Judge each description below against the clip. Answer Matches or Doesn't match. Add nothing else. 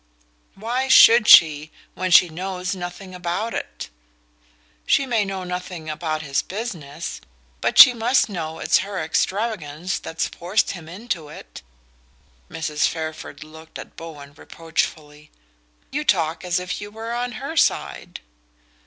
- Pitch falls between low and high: Matches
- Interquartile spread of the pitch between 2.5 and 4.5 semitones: Doesn't match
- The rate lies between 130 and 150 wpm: Matches